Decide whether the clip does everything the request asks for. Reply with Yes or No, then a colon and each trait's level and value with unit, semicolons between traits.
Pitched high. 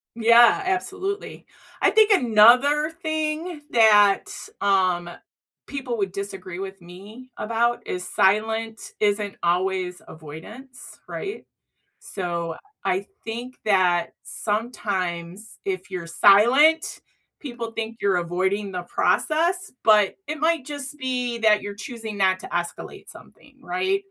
Yes: high, 220 Hz